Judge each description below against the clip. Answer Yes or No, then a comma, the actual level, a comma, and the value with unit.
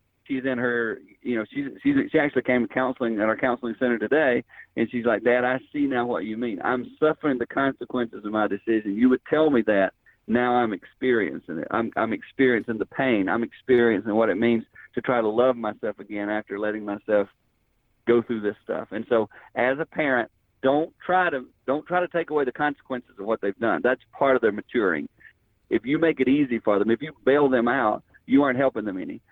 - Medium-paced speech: No, fast, 220 wpm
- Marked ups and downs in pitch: No, average, 3.3 semitones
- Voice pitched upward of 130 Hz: No, low, 125 Hz